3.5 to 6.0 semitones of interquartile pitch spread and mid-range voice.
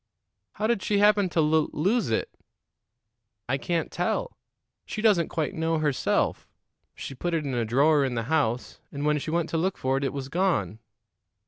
Yes: average, 4.6 semitones; medium, 155 Hz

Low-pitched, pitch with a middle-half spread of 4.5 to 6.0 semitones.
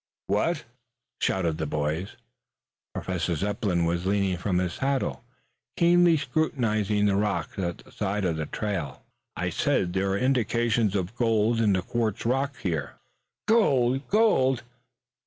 Yes: low, 105 Hz; wide, 5.5 semitones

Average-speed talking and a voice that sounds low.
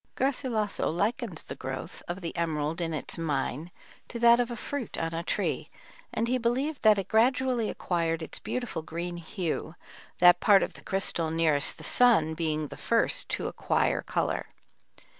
No: average, 170 wpm; medium, 180 Hz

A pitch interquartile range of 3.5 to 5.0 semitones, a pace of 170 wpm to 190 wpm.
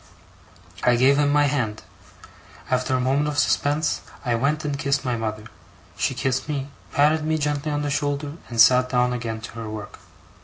No: average, 3.1 semitones; average, 185 wpm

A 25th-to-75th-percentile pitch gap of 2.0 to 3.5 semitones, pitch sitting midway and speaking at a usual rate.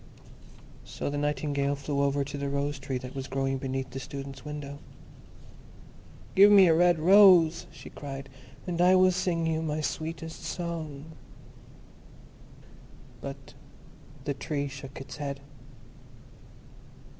No: average, 3.0 semitones; medium, 145 Hz; slow, 130 wpm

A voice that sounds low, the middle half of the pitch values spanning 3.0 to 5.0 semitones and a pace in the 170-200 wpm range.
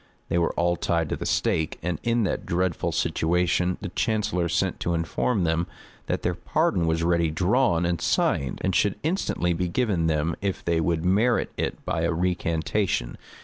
No: very low, 85 Hz; narrow, 2.5 semitones; average, 180 wpm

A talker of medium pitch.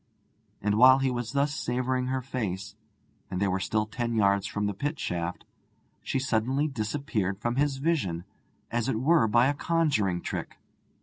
No: low, 120 Hz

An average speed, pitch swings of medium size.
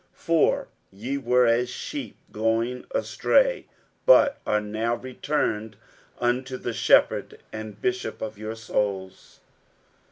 No: slow, 120 wpm; average, 3.3 semitones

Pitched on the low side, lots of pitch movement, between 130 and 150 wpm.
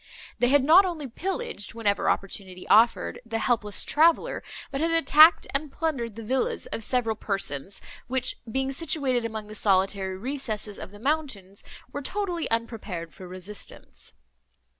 No: high, 230 Hz; wide, 6.0 semitones; average, 145 wpm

